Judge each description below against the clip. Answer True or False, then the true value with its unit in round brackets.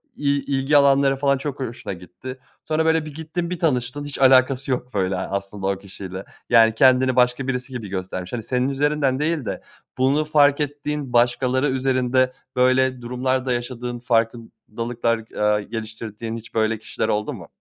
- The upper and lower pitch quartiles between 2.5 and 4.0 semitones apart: True (3.4 semitones)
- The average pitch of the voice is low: True (125 Hz)